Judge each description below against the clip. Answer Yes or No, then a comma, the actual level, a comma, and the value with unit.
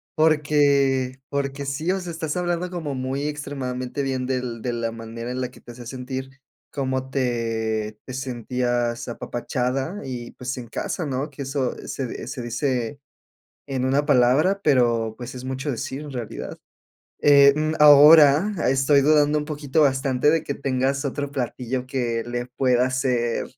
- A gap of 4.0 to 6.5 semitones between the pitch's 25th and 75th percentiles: No, narrow, 2.6 semitones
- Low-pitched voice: Yes, low, 130 Hz